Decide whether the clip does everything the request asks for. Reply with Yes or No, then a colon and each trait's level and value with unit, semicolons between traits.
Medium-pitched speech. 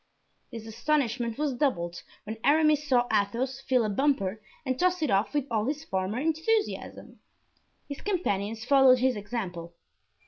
No: very high, 250 Hz